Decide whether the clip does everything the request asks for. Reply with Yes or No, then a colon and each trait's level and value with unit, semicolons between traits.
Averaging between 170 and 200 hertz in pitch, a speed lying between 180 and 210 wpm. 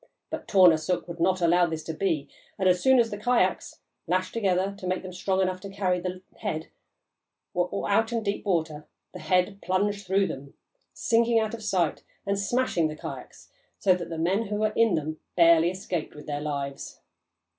Yes: medium, 185 Hz; average, 190 wpm